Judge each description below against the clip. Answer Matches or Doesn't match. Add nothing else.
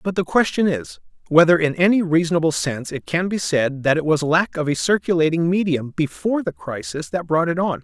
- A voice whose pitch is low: Doesn't match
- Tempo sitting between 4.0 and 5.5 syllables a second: Doesn't match